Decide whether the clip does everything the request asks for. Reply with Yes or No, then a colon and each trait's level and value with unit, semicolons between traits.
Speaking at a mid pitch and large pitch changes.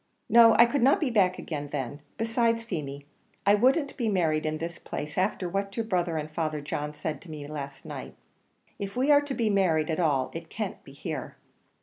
Yes: medium, 180 Hz; wide, 6.9 semitones